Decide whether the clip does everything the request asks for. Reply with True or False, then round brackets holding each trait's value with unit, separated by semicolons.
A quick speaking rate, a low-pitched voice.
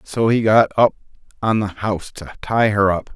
True (210 wpm; 105 Hz)